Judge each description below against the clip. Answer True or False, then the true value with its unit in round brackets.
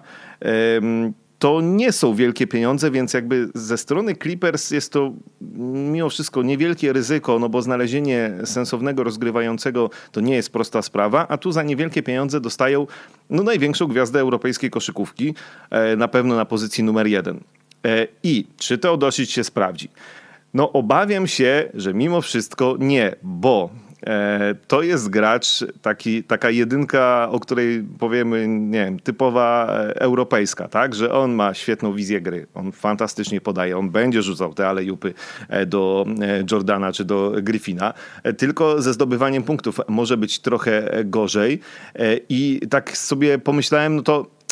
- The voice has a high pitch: False (125 Hz)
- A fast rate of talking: False (140 wpm)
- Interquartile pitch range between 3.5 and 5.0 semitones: True (4.2 semitones)